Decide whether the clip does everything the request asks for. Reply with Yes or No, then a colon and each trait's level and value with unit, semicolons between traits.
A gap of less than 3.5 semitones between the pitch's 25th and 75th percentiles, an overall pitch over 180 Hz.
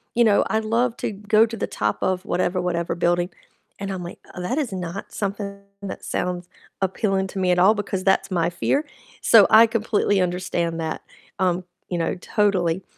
Yes: average, 2.8 semitones; high, 190 Hz